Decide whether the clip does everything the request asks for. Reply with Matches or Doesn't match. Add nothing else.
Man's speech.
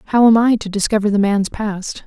Doesn't match